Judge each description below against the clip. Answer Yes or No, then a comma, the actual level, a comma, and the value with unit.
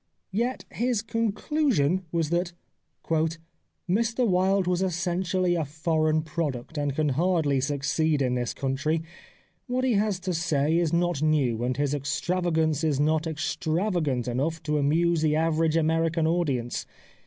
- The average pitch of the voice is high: No, medium, 160 Hz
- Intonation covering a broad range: No, average, 3.5 semitones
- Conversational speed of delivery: Yes, average, 145 wpm